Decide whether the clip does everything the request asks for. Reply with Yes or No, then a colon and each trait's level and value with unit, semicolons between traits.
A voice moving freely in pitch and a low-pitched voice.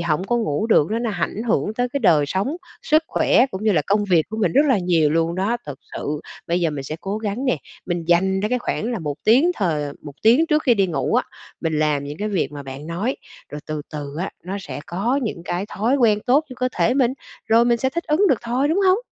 No: wide, 6.9 semitones; high, 200 Hz